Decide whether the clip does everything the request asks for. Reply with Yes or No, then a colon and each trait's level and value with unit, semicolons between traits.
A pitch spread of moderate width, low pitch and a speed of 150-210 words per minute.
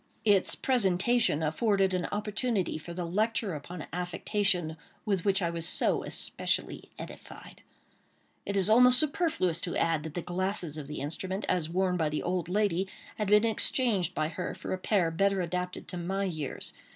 No: average, 3.5 semitones; medium, 185 Hz; average, 170 wpm